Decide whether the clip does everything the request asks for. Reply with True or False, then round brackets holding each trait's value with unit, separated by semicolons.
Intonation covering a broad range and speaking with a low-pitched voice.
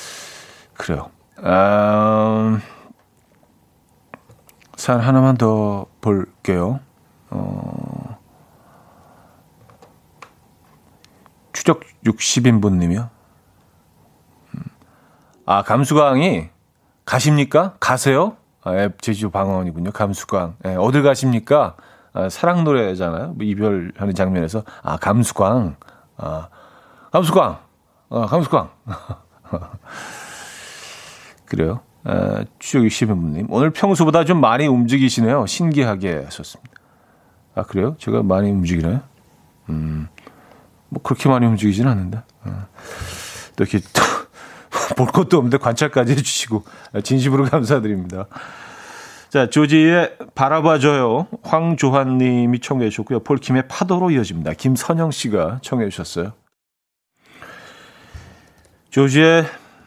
True (6.0 semitones; 115 Hz)